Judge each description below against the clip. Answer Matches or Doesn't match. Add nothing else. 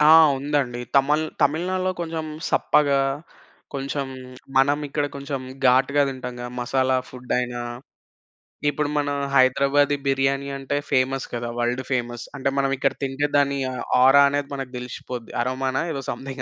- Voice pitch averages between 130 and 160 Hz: Matches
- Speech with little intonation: Matches